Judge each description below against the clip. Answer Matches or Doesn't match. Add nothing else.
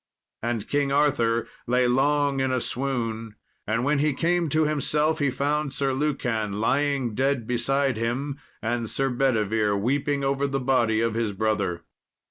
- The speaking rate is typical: Matches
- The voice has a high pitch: Doesn't match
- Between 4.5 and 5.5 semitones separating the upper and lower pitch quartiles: Doesn't match